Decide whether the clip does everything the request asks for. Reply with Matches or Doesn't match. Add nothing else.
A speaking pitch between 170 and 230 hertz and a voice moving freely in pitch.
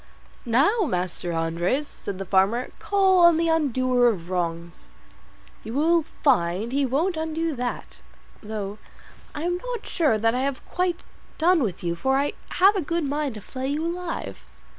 Doesn't match